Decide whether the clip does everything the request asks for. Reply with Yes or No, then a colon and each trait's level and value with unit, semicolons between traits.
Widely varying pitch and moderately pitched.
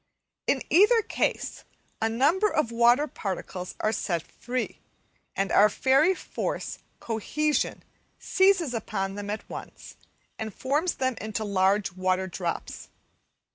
No: wide, 7.1 semitones; high, 225 Hz